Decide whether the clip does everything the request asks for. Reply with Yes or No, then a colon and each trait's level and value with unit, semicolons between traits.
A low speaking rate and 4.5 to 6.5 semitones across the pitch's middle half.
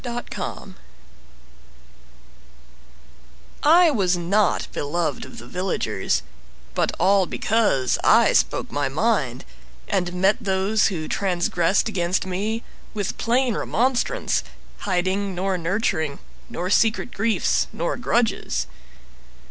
No: slow, 105 wpm; average, 4.0 semitones